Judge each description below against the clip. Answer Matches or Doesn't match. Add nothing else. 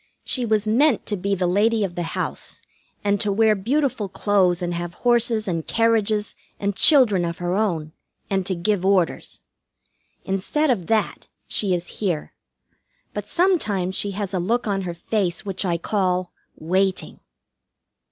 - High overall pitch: Matches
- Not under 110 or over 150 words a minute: Doesn't match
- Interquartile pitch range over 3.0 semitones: Matches